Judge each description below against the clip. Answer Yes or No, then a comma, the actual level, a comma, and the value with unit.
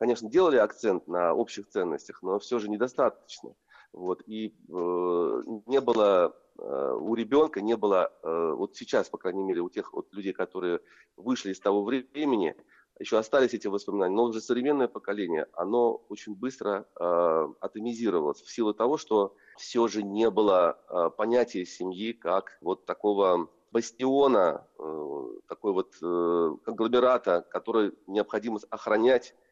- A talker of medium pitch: No, low, 115 Hz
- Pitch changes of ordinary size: Yes, average, 4.5 semitones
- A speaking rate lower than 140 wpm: No, average, 145 wpm